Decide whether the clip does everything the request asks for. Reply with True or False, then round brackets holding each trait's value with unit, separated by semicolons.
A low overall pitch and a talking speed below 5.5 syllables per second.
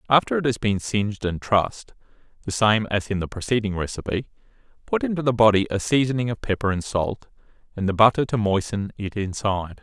False (105 Hz; 5.9 syllables/s)